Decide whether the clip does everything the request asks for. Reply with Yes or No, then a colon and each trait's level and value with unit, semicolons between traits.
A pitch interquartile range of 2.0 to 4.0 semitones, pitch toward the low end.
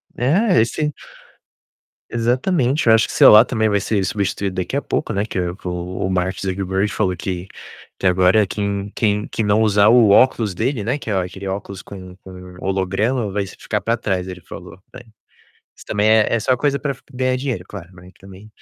Yes: average, 3.5 semitones; low, 100 Hz